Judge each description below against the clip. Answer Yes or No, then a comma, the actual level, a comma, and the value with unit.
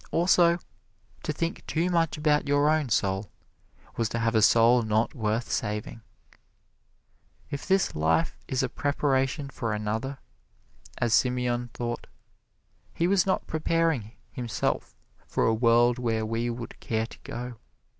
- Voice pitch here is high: No, low, 120 Hz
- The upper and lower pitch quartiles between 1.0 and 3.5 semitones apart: No, average, 4.7 semitones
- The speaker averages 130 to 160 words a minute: Yes, average, 140 wpm